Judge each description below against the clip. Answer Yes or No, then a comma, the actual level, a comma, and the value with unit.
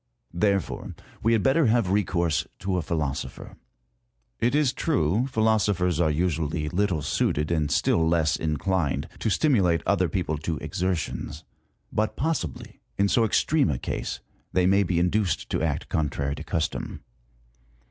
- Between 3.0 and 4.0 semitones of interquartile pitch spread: No, average, 4.9 semitones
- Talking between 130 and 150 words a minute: Yes, average, 145 wpm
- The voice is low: Yes, very low, 90 Hz